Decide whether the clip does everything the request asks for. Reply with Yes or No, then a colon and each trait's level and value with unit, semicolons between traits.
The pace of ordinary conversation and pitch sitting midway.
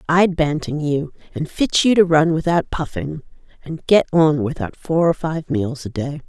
Yes: average, 190 wpm; medium, 155 Hz